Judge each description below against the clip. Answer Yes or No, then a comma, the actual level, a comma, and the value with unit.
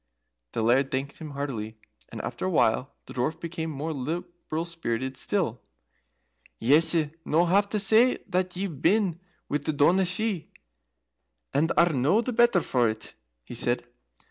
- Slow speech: No, average, 155 wpm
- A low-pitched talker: No, medium, 160 Hz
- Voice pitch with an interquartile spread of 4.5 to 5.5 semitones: Yes, average, 5.0 semitones